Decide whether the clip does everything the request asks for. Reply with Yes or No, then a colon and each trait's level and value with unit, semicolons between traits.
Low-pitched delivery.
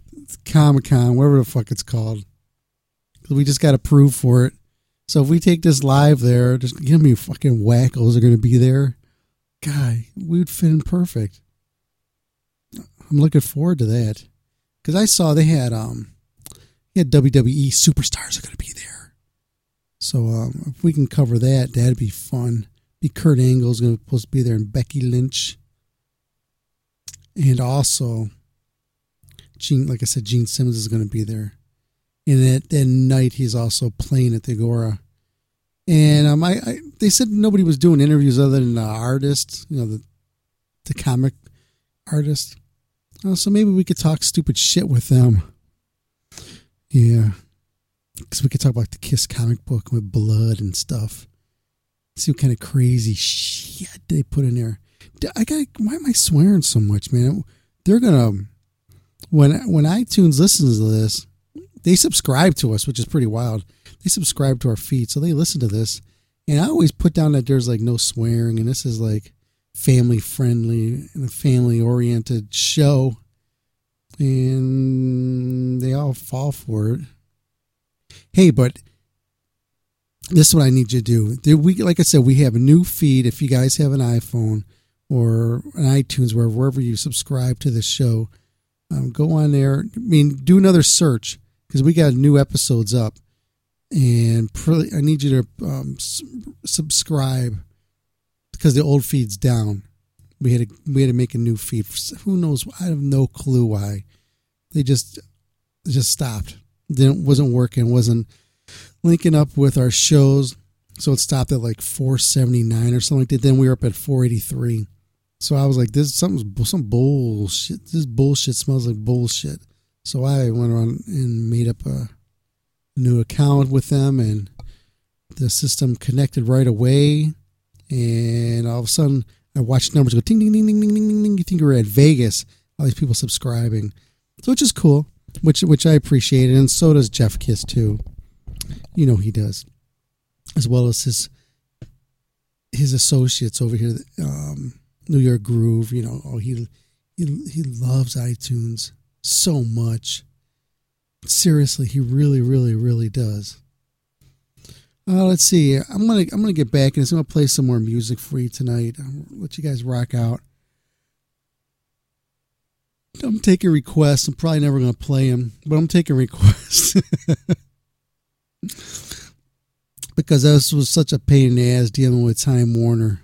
Yes: low, 125 Hz